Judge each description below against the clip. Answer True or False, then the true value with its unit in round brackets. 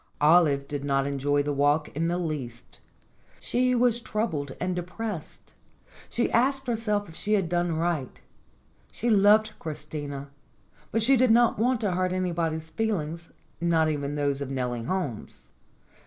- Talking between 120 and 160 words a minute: True (150 wpm)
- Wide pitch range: True (6.7 semitones)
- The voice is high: False (170 Hz)